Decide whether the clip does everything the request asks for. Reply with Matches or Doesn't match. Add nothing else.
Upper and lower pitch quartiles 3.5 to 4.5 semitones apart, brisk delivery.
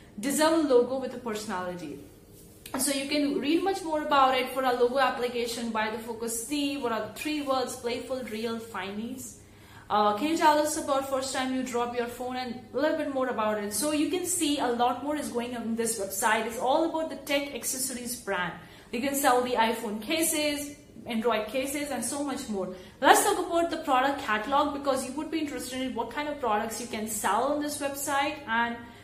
Matches